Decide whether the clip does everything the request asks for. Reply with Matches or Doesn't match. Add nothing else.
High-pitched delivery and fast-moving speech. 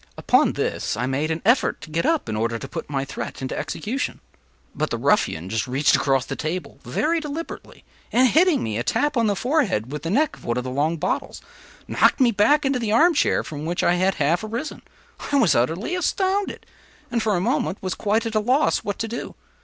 Matches